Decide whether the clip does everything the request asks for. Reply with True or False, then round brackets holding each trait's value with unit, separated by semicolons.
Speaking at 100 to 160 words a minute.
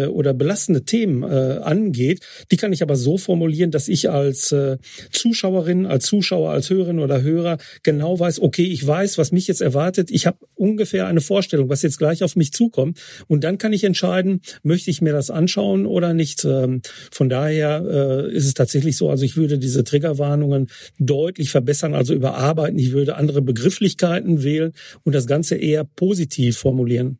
False (170 wpm)